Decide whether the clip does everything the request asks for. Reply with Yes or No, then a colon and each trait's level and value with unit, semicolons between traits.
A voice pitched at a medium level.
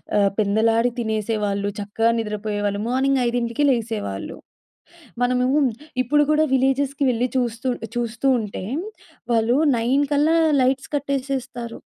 No: high, 235 Hz